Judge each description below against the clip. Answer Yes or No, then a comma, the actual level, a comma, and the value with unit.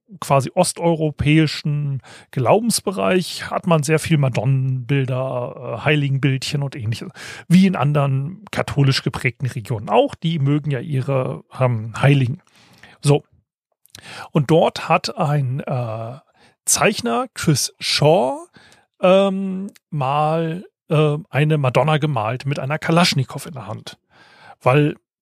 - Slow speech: Yes, slow, 110 wpm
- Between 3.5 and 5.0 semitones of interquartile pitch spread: Yes, average, 3.8 semitones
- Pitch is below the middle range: No, medium, 145 Hz